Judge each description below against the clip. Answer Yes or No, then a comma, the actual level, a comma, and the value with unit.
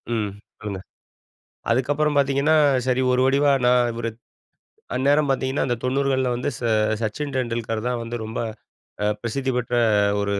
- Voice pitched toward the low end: Yes, low, 125 Hz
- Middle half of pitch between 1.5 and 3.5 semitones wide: Yes, average, 2.8 semitones